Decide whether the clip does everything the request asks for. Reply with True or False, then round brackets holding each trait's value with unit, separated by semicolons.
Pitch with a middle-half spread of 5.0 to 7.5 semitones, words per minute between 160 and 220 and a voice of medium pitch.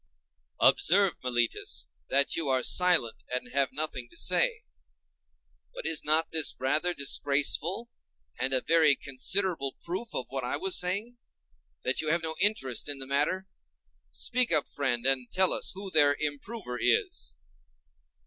False (5.3 semitones; 150 wpm; 150 Hz)